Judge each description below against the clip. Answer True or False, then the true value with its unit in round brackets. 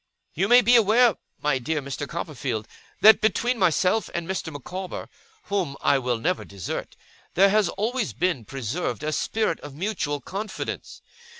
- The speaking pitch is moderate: True (180 Hz)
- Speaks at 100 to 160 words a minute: True (155 wpm)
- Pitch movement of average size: False (6.9 semitones)